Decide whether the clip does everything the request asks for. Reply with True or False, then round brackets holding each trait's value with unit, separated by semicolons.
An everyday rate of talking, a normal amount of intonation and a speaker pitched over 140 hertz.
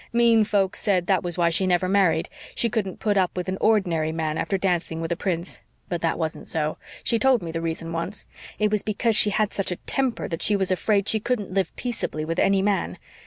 False (230 wpm; 4.0 semitones; 190 Hz)